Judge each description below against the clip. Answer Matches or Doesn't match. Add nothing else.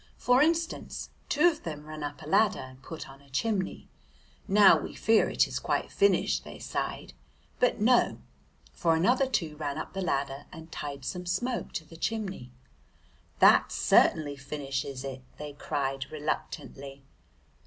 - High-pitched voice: Doesn't match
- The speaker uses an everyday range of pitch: Doesn't match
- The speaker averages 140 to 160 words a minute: Matches